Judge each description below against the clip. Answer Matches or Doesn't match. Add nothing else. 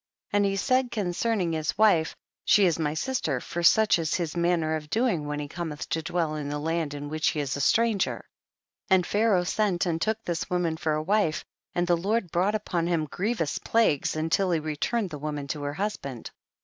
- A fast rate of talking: Matches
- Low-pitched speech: Doesn't match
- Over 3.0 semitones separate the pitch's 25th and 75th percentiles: Matches